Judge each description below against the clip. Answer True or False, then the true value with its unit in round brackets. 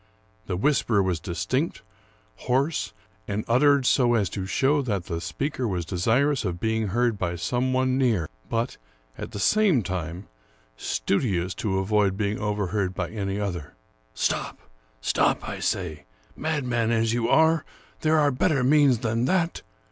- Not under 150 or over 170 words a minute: True (155 wpm)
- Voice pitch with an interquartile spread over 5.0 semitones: True (5.6 semitones)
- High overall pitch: False (110 Hz)